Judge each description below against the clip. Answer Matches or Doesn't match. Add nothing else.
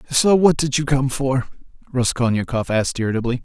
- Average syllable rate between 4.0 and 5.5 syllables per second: Doesn't match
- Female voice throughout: Doesn't match